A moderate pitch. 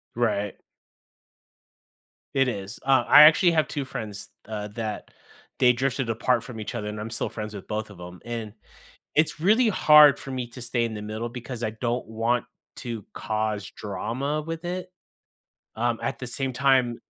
No: low, 120 Hz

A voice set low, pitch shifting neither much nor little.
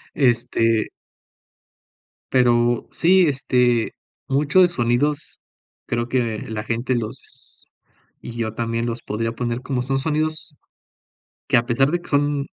Yes: low, 125 Hz; average, 3.4 semitones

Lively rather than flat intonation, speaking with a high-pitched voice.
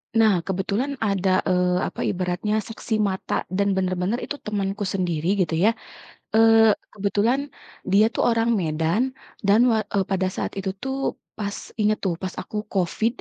No: average, 3.0 semitones; high, 200 Hz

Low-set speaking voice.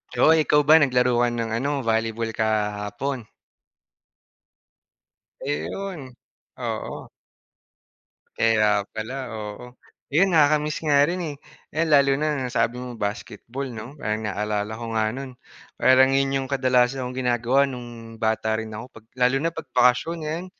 Yes: low, 125 Hz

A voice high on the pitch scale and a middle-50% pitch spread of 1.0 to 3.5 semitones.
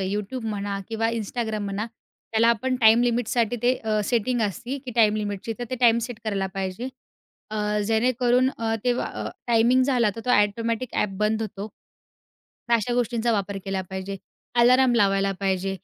Yes: high, 225 Hz; average, 2.9 semitones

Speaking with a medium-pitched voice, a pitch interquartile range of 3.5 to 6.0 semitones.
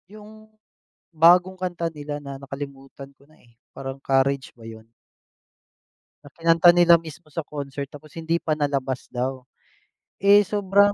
Yes: medium, 150 Hz; average, 4.1 semitones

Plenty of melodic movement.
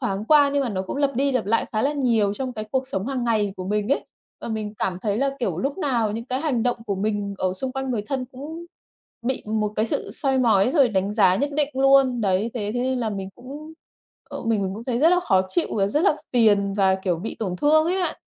No: average, 4.9 semitones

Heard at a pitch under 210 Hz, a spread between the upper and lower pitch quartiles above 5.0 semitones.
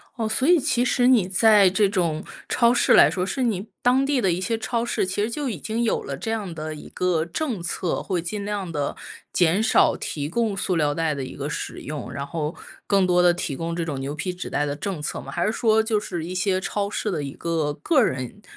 Yes: medium, 185 Hz; wide, 5.5 semitones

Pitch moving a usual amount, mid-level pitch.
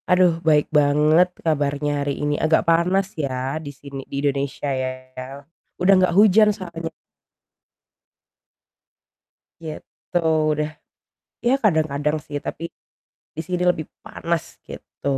Yes: average, 3.1 semitones; medium, 155 Hz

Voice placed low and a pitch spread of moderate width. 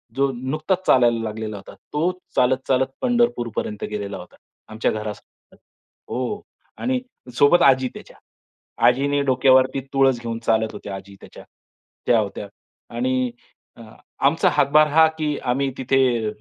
Yes: low, 130 Hz; average, 4.2 semitones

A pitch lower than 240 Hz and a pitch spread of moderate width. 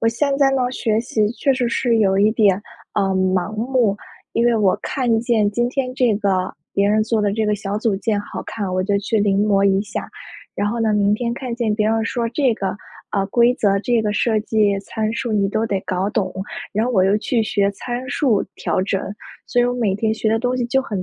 Yes: high, 215 Hz; average, 3.0 semitones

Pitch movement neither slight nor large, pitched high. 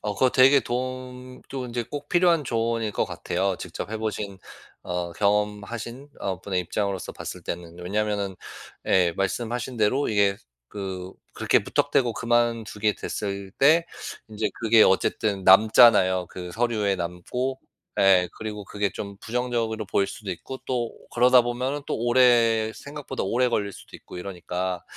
No: average, 3.9 semitones; low, 110 Hz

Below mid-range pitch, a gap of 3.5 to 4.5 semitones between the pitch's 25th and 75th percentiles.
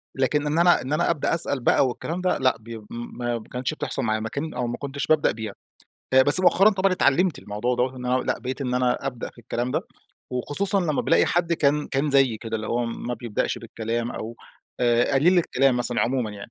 Yes: low, 130 Hz; average, 4.0 semitones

